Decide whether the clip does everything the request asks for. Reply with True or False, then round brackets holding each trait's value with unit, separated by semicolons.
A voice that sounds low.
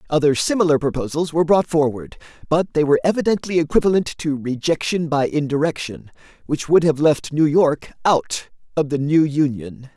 False (150 Hz)